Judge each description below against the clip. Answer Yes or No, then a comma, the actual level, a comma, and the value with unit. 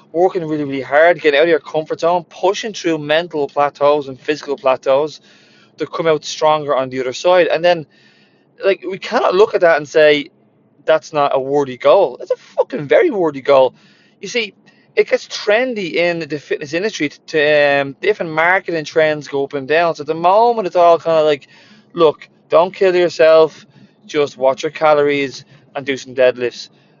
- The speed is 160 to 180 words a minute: No, average, 190 wpm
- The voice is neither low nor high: Yes, medium, 155 Hz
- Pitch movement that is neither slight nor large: Yes, average, 3.9 semitones